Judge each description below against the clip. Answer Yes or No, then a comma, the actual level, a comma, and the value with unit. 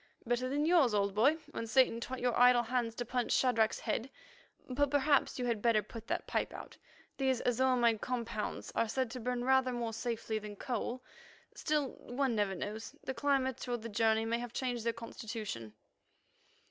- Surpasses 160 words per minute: Yes, average, 185 wpm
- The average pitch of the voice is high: Yes, high, 240 Hz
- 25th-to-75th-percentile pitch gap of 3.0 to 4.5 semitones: No, narrow, 2.5 semitones